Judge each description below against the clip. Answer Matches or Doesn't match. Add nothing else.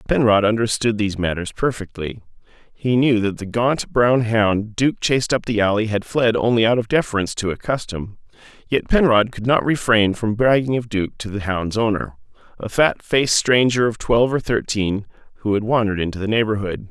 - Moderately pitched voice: Doesn't match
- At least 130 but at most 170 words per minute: Doesn't match